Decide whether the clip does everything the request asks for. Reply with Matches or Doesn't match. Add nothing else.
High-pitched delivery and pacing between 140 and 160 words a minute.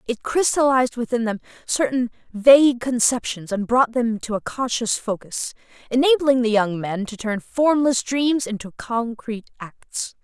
Matches